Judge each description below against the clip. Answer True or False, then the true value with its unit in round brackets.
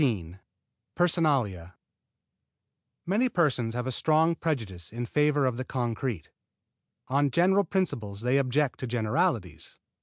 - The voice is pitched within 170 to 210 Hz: False (130 Hz)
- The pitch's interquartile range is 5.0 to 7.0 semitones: True (5.6 semitones)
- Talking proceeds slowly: True (120 wpm)